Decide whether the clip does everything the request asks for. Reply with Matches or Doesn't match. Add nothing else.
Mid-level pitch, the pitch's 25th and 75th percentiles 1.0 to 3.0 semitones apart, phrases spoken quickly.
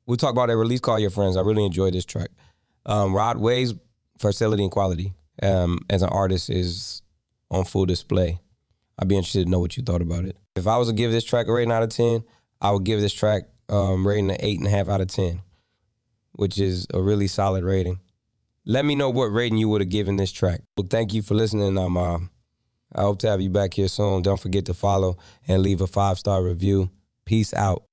Doesn't match